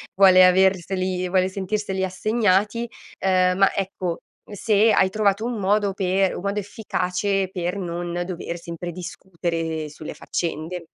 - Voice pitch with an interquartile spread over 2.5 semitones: No, narrow, 2.0 semitones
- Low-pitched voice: No, medium, 185 Hz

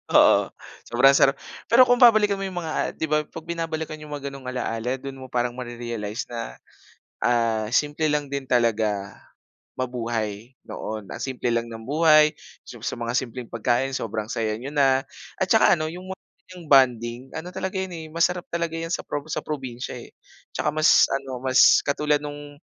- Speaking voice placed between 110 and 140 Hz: Yes, low, 135 Hz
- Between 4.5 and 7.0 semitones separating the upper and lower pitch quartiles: Yes, average, 4.8 semitones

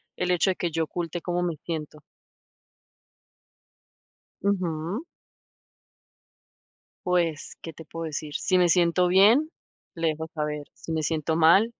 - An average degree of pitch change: No, narrow, 2.2 semitones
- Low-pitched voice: No, medium, 170 Hz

